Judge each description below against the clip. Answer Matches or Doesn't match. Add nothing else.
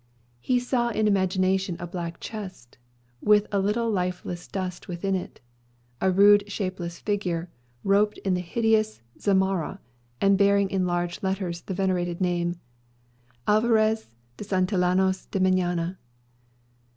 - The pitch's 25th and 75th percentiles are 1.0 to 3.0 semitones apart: Matches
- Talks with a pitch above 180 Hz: Matches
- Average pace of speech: Doesn't match